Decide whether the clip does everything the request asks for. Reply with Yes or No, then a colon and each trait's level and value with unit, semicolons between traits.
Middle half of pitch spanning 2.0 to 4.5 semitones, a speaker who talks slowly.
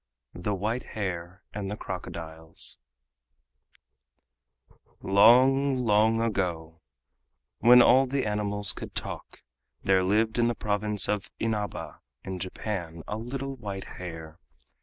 Yes: average, 3.8 semitones; slow, 115 wpm